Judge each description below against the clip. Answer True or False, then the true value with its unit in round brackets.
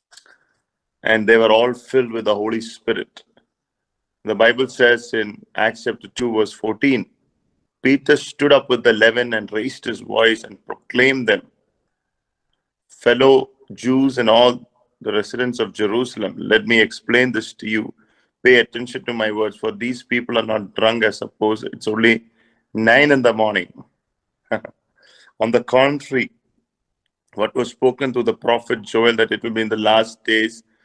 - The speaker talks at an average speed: True (160 wpm)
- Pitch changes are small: True (2.2 semitones)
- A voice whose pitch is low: True (115 Hz)